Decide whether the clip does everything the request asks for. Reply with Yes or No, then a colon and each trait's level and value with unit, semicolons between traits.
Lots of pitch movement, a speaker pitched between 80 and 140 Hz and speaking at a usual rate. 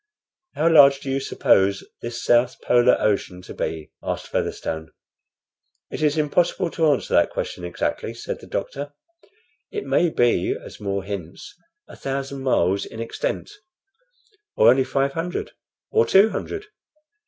Yes: wide, 7.1 semitones; low, 135 Hz; average, 145 wpm